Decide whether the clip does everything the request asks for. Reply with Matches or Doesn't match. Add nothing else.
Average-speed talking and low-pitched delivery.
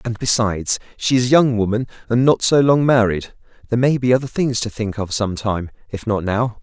Doesn't match